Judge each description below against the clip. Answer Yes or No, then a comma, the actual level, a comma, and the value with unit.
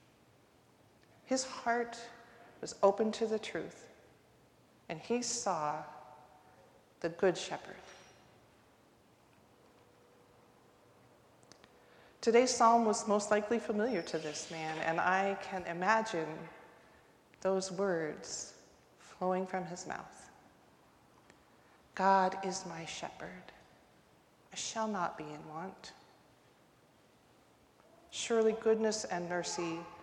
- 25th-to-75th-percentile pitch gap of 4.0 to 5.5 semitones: Yes, average, 4.9 semitones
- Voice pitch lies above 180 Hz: Yes, high, 190 Hz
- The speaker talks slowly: Yes, slow, 90 wpm